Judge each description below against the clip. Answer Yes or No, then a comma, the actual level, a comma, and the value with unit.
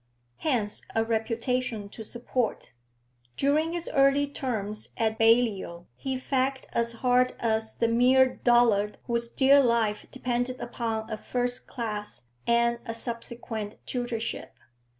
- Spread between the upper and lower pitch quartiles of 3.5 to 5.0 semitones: No, narrow, 2.4 semitones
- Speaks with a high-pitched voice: Yes, high, 235 Hz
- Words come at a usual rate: No, slow, 125 wpm